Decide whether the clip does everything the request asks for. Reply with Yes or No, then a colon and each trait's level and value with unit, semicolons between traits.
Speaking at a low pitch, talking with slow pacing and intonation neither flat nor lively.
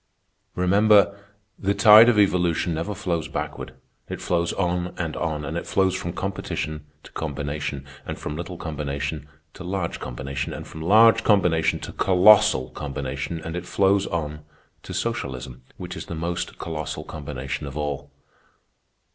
No: very low, 85 Hz; average, 150 wpm; average, 4.6 semitones